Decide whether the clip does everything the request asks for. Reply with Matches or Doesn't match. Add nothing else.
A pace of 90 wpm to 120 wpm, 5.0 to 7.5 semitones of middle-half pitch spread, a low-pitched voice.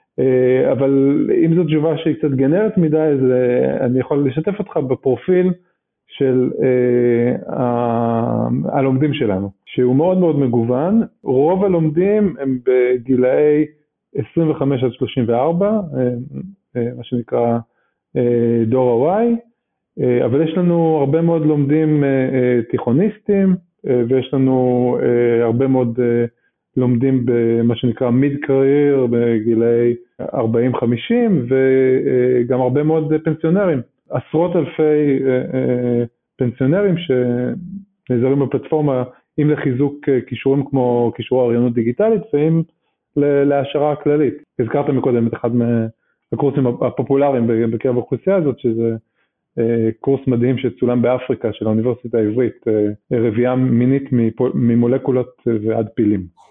Doesn't match